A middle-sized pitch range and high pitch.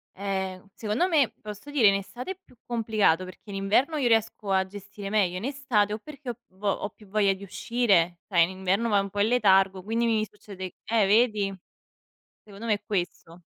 Yes: average, 3.1 semitones; high, 205 Hz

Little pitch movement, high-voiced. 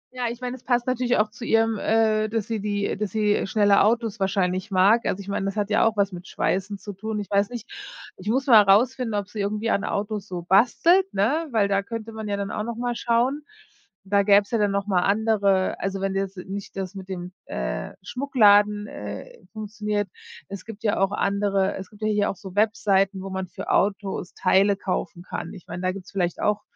Yes: narrow, 2.3 semitones; high, 205 Hz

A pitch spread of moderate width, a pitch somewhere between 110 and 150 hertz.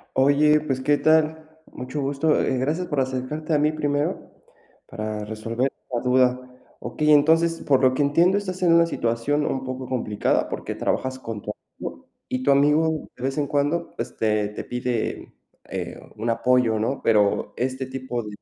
Yes: average, 3.6 semitones; low, 135 Hz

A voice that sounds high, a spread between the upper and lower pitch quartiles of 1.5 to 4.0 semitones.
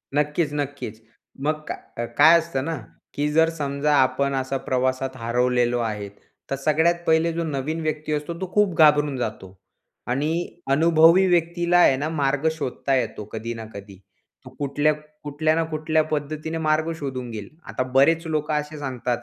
No: medium, 150 Hz; average, 3.5 semitones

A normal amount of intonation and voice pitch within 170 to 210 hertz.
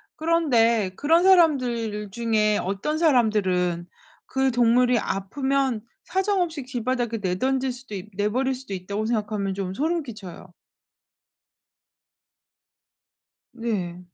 No: average, 4.8 semitones; high, 235 Hz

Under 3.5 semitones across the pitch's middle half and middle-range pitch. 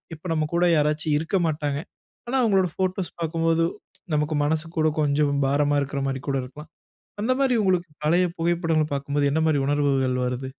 Yes: average, 2.8 semitones; medium, 155 Hz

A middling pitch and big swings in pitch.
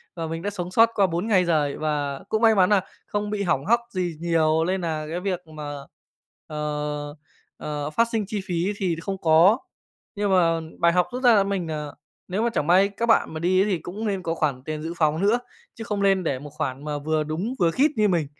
No: medium, 175 Hz; average, 4.5 semitones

